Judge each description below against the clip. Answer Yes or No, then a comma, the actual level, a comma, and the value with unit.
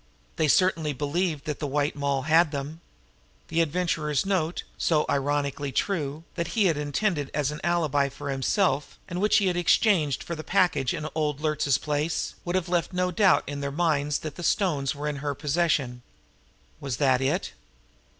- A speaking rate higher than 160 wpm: Yes, average, 180 wpm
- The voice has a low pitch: No, medium, 150 Hz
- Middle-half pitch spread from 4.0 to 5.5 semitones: No, average, 3.5 semitones